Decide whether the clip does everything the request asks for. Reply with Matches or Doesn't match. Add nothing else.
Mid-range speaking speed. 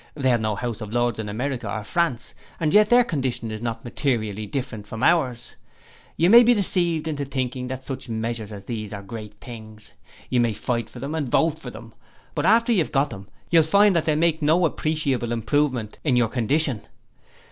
Doesn't match